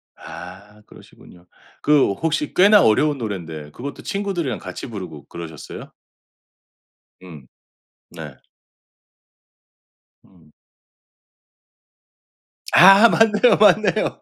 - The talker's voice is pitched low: Yes, low, 125 Hz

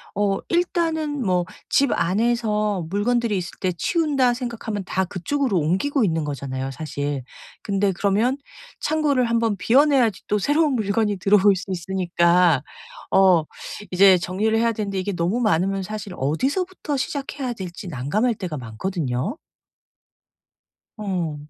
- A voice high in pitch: Yes, high, 200 Hz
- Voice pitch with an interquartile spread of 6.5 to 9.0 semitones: No, wide, 5.5 semitones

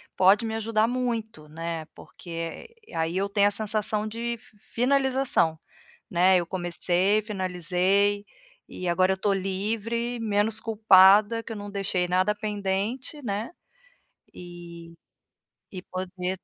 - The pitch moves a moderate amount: Yes, average, 3.5 semitones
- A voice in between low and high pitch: No, high, 200 Hz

